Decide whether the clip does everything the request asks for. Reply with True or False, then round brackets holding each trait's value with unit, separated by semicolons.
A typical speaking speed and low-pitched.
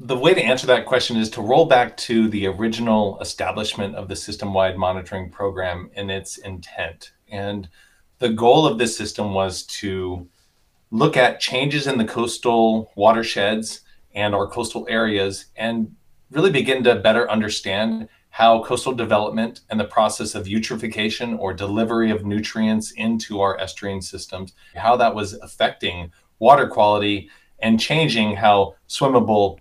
True (150 wpm; 105 Hz)